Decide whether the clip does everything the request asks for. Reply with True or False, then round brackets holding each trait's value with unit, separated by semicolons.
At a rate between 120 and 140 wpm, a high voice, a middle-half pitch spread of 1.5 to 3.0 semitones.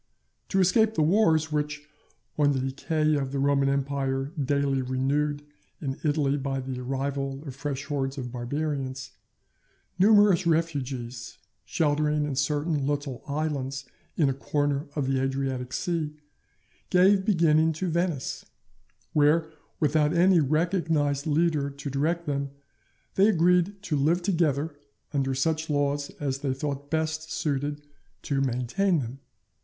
False (135 wpm; 145 Hz; 2.7 semitones)